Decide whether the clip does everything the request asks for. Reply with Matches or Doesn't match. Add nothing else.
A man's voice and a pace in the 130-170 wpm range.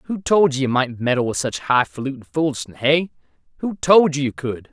Doesn't match